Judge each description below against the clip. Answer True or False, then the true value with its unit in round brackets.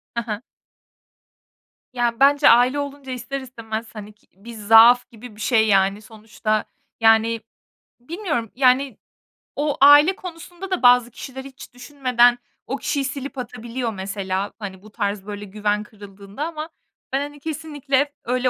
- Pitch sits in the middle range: False (245 Hz)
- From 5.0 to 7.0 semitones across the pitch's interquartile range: False (4.5 semitones)